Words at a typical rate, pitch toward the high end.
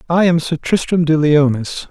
No: average, 190 wpm; medium, 160 Hz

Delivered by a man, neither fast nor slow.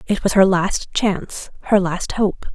No: female; average, 190 wpm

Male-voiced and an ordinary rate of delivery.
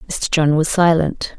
No: female; average, 175 wpm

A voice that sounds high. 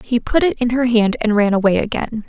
Yes: high, 230 Hz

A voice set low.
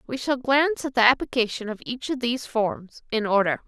No: high, 240 Hz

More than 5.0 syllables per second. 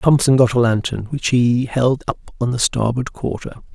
No: 4.9 syllables/s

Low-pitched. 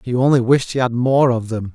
Yes: low, 125 Hz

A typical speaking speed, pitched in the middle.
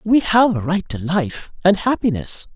Yes: average, 165 wpm; medium, 180 Hz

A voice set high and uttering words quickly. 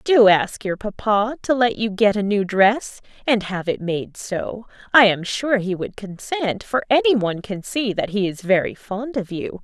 Yes: high, 210 Hz; fast, 210 wpm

